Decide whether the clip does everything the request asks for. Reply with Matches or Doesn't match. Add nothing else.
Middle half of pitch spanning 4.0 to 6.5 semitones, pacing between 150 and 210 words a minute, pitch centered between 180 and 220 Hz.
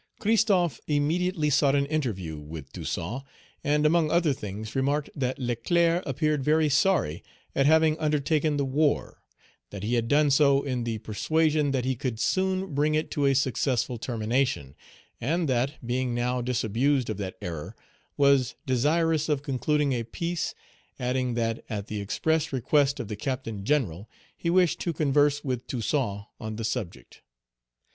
Doesn't match